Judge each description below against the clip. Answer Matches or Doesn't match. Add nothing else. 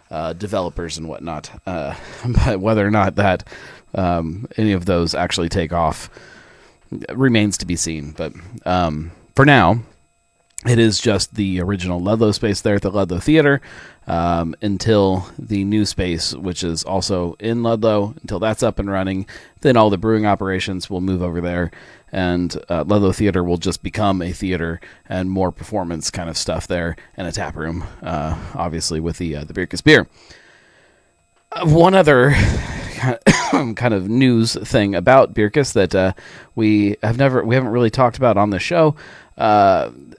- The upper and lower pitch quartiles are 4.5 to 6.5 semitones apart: Doesn't match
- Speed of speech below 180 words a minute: Matches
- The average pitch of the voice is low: Matches